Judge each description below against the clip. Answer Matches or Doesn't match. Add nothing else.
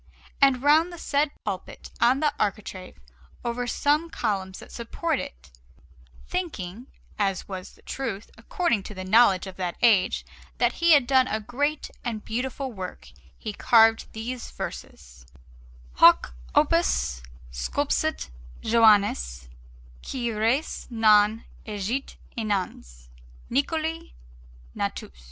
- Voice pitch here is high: Matches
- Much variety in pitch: Matches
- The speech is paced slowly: Matches